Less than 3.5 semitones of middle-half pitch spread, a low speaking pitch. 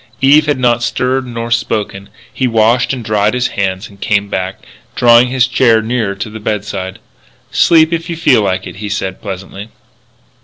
No: average, 3.9 semitones; low, 115 Hz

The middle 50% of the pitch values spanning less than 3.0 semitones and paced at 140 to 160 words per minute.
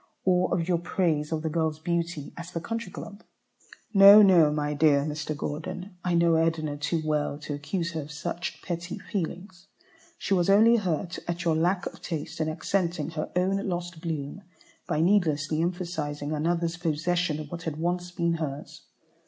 No: narrow, 2.6 semitones; average, 175 wpm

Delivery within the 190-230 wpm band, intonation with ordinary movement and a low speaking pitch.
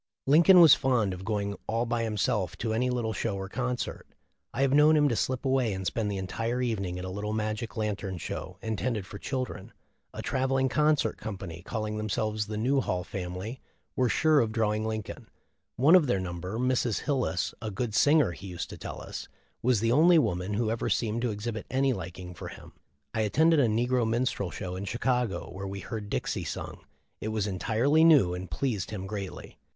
Yes: average, 200 wpm; average, 4.4 semitones; low, 110 Hz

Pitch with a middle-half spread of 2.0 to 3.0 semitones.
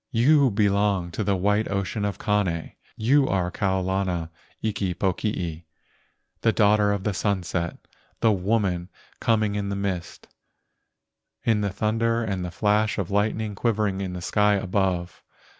Yes: narrow, 2.5 semitones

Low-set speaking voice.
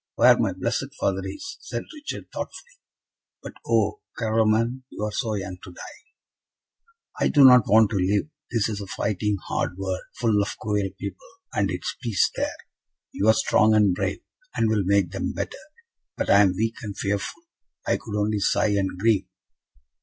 Yes: low, 105 Hz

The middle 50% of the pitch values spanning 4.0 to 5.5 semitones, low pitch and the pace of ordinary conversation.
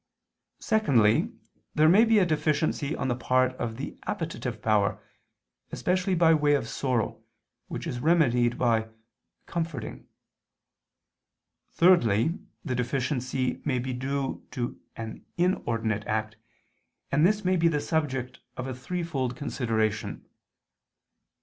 No: average, 5.2 semitones; low, 130 Hz; slow, 125 wpm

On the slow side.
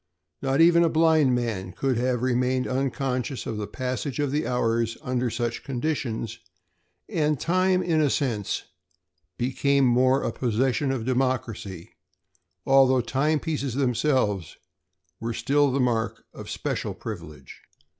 Yes: slow, 130 wpm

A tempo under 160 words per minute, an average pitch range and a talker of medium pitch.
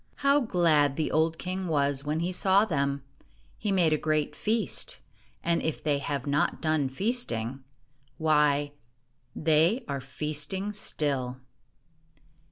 Yes: slow, 135 wpm; average, 4.3 semitones; medium, 155 Hz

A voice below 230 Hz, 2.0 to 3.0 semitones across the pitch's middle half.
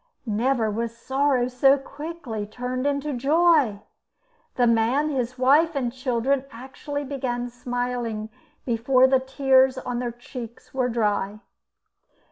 No: very high, 255 Hz; narrow, 2.6 semitones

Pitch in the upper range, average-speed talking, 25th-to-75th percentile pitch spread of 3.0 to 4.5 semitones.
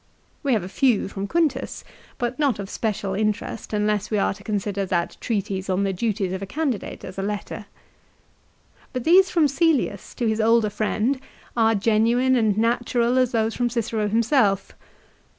Yes: high, 220 Hz; average, 170 wpm; average, 3.5 semitones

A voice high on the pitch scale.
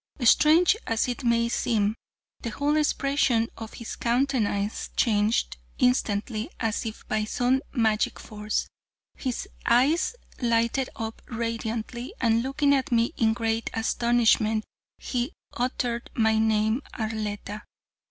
Yes: high, 230 Hz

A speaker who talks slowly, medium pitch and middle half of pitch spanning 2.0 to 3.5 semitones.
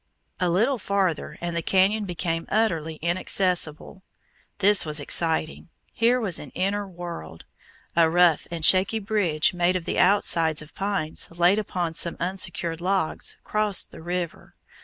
No: average, 145 wpm; medium, 175 Hz; average, 3.0 semitones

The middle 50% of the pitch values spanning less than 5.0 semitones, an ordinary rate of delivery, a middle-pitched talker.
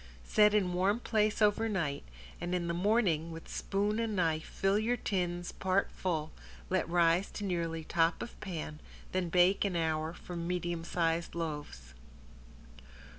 Yes: average, 3.2 semitones; average, 155 wpm; medium, 175 Hz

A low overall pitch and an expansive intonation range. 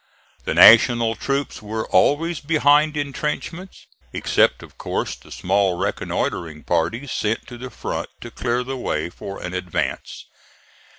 Yes: low, 120 Hz; wide, 6.5 semitones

